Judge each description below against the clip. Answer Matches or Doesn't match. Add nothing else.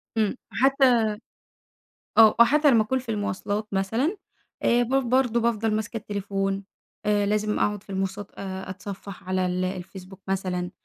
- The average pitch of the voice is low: Doesn't match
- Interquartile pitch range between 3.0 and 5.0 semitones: Matches